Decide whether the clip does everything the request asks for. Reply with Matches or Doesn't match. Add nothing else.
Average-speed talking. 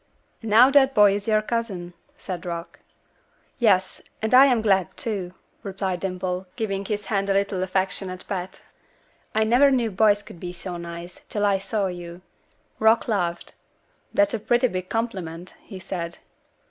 Matches